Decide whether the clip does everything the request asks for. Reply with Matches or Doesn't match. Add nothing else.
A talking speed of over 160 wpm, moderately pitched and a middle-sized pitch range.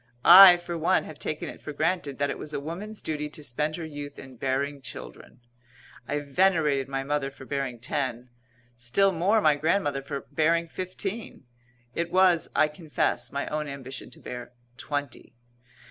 Matches